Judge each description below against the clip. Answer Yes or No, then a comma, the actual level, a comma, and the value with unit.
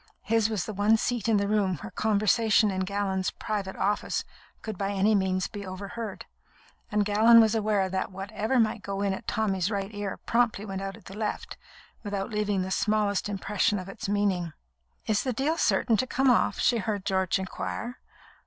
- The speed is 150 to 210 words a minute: Yes, average, 190 wpm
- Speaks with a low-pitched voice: No, high, 205 Hz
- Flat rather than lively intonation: Yes, narrow, 2.1 semitones